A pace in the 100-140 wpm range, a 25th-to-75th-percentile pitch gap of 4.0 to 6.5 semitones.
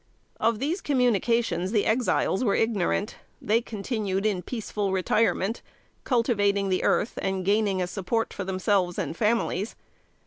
No: slow, 135 wpm; average, 3.3 semitones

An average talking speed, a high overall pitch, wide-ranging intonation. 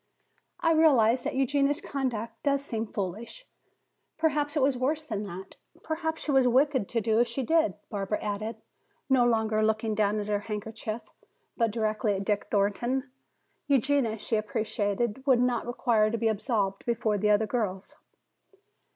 No: average, 160 wpm; high, 230 Hz; average, 4.0 semitones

